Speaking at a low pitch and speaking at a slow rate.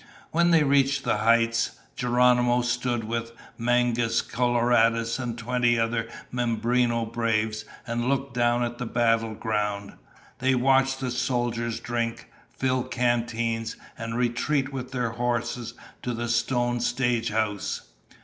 Yes: low, 120 Hz; slow, 125 wpm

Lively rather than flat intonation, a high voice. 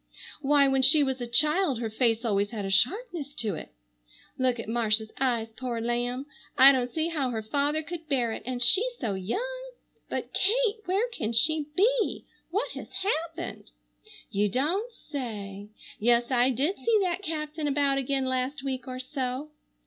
No: average, 5.0 semitones; very high, 265 Hz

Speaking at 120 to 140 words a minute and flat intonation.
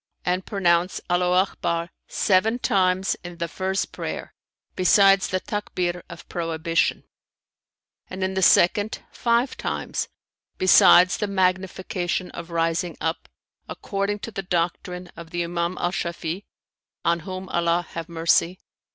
Yes: slow, 135 wpm; narrow, 1.9 semitones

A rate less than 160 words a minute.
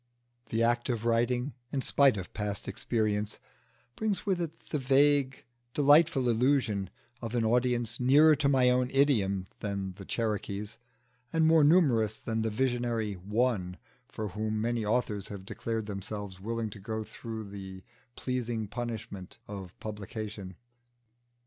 Yes: slow, 135 wpm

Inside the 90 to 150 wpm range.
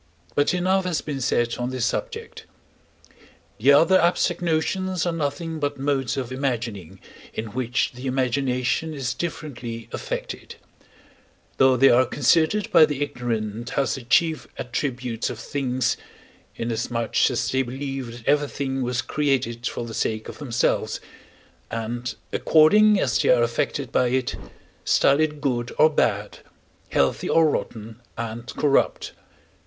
Yes: average, 140 wpm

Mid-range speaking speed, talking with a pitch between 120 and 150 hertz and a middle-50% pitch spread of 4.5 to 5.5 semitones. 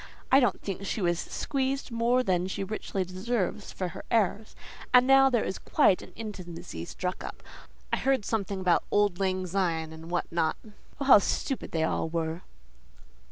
No: average, 175 wpm; high, 190 Hz; average, 4.9 semitones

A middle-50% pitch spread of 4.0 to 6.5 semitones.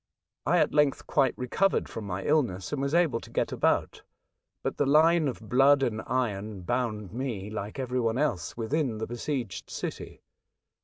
Yes: average, 4.8 semitones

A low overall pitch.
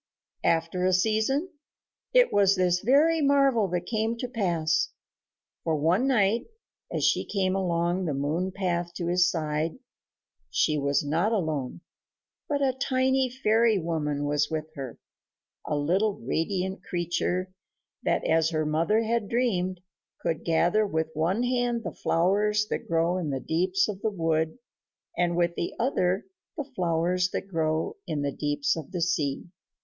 No: medium, 180 Hz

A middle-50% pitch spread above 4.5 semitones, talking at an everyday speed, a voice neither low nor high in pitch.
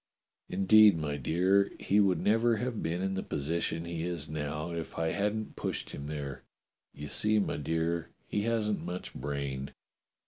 No: average, 5.2 semitones; average, 165 wpm; very low, 85 Hz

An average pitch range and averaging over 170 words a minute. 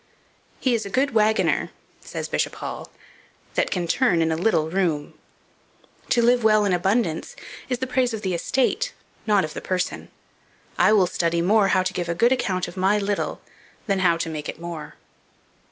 Yes: average, 4.7 semitones; average, 185 wpm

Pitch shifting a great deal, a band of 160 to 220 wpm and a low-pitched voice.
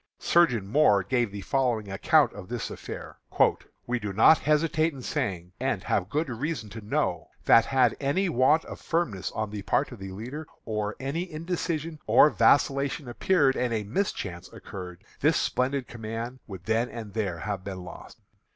Yes: wide, 6.2 semitones; average, 170 wpm; low, 120 Hz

